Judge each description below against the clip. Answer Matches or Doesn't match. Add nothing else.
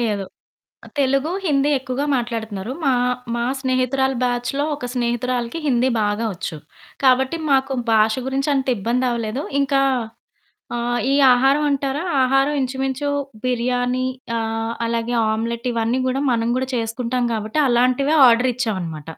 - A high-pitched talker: Matches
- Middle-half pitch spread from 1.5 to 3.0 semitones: Matches